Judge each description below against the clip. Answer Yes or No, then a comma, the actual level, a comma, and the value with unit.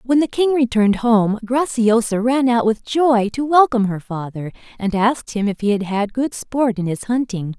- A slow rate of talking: No, fast, 205 wpm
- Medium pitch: No, high, 230 Hz